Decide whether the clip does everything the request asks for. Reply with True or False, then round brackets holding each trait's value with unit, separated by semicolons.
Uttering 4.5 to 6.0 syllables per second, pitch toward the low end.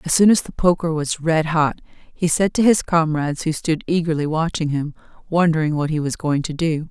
False (5.3 syllables/s; 160 Hz)